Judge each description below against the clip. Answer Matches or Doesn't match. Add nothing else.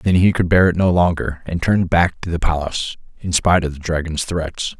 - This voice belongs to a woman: Doesn't match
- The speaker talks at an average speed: Doesn't match